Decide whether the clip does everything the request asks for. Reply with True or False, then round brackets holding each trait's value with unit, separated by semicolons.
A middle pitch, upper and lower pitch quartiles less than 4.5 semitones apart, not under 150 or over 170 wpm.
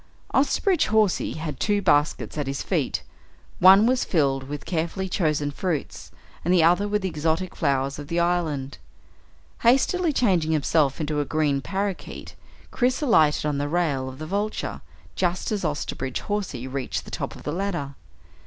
False (165 Hz; 5.4 semitones; 165 wpm)